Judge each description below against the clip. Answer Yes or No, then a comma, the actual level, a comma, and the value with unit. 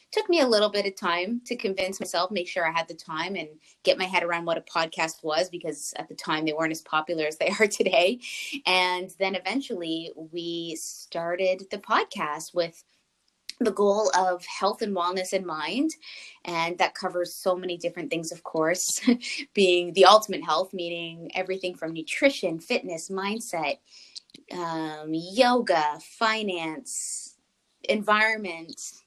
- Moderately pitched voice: Yes, medium, 180 Hz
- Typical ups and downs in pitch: Yes, average, 3.3 semitones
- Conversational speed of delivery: Yes, average, 155 wpm